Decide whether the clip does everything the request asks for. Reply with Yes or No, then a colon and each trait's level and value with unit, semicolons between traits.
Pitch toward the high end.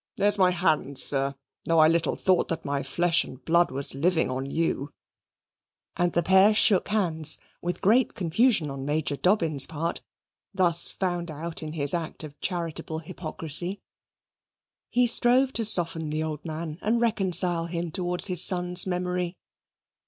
No: medium, 170 Hz